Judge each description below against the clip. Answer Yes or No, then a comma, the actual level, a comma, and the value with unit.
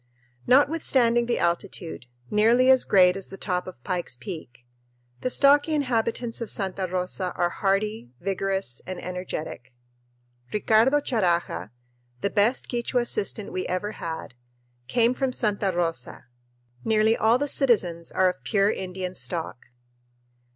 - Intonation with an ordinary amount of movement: Yes, average, 4.7 semitones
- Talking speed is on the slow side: Yes, slow, 130 wpm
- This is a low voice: No, high, 195 Hz